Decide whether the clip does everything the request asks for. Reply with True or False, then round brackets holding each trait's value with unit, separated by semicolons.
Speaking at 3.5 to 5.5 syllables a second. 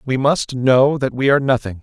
True (5.3 syllables/s)